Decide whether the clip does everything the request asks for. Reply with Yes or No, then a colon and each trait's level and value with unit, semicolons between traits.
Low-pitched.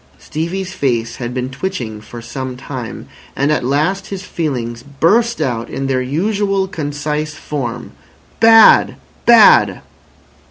No: medium, 145 Hz